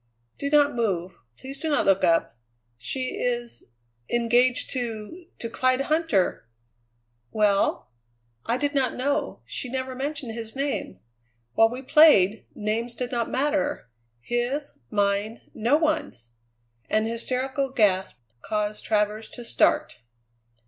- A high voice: Yes, high, 240 Hz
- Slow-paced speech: Yes, slow, 125 wpm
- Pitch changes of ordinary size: Yes, average, 4.3 semitones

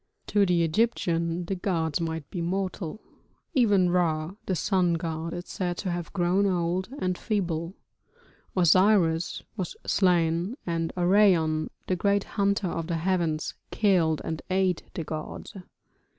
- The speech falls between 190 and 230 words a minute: No, slow, 135 wpm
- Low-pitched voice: No, medium, 175 Hz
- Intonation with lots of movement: No, narrow, 2.6 semitones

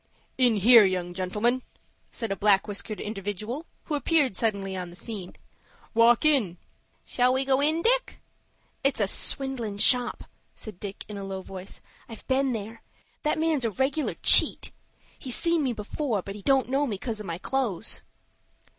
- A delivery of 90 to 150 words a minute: No, average, 170 wpm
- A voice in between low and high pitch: No, high, 225 Hz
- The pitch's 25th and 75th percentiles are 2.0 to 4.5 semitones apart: No, average, 5.2 semitones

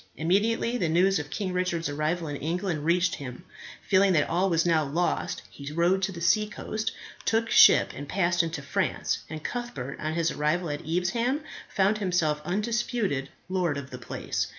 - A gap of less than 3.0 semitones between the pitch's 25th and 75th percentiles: No, average, 4.1 semitones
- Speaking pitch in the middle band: Yes, medium, 175 Hz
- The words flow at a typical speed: Yes, average, 175 wpm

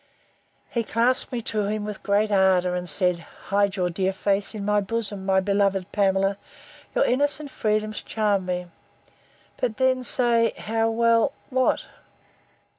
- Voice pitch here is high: Yes, high, 210 Hz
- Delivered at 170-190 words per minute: No, slow, 135 wpm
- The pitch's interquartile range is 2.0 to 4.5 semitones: Yes, average, 3.2 semitones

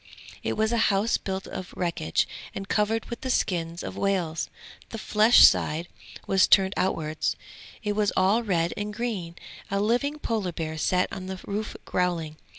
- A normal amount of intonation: Yes, average, 3.7 semitones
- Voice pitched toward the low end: No, high, 195 Hz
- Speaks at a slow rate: No, average, 165 wpm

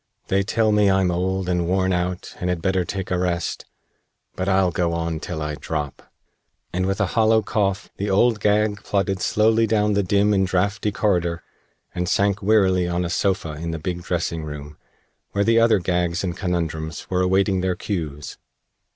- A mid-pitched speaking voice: No, very low, 95 Hz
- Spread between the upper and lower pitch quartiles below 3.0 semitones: Yes, narrow, 2.5 semitones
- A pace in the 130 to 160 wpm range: No, average, 185 wpm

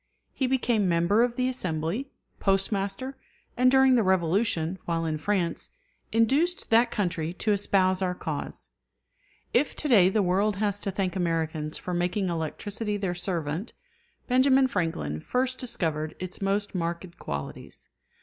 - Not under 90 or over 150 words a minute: Yes, average, 140 wpm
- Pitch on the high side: Yes, high, 195 Hz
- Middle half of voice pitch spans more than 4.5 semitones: Yes, average, 5.1 semitones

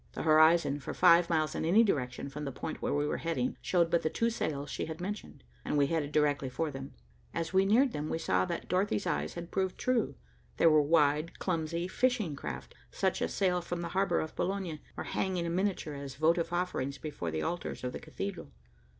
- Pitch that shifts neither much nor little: Yes, average, 3.9 semitones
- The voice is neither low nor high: Yes, medium, 165 Hz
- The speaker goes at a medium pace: No, fast, 215 wpm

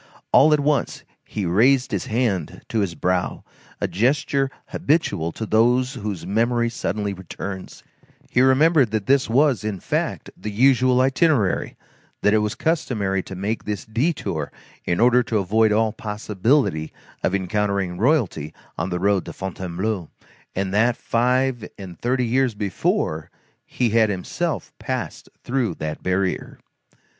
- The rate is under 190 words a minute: Yes, average, 145 wpm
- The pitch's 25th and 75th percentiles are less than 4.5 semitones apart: No, average, 4.8 semitones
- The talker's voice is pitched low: Yes, low, 110 Hz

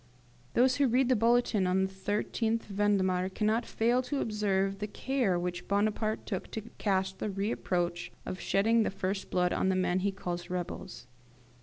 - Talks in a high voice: Yes, high, 200 Hz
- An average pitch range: Yes, average, 3.1 semitones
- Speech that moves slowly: No, average, 170 wpm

